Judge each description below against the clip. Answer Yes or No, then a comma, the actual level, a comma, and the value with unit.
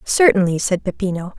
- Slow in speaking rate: Yes, slow, 130 wpm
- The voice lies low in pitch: No, high, 195 Hz